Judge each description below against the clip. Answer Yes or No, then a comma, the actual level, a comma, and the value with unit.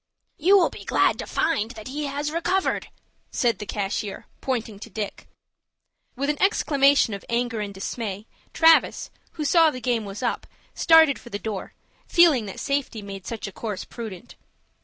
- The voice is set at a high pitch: Yes, high, 240 Hz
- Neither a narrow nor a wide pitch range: No, wide, 6.0 semitones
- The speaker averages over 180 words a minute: No, average, 170 wpm